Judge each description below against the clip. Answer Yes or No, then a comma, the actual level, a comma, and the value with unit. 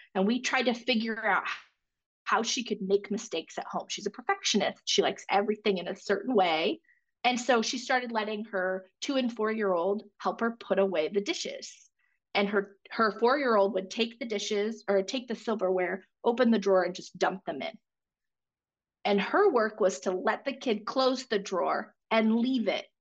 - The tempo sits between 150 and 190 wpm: No, average, 200 wpm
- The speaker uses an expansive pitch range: No, average, 4.0 semitones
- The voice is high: Yes, high, 220 Hz